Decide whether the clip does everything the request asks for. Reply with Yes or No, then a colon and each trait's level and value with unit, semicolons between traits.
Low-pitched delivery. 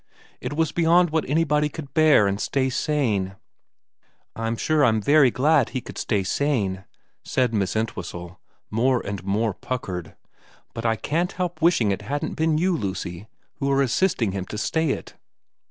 Yes: low, 130 Hz